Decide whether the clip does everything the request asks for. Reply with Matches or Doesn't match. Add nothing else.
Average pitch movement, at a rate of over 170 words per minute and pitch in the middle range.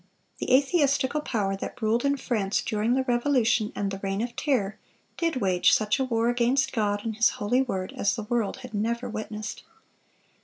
Doesn't match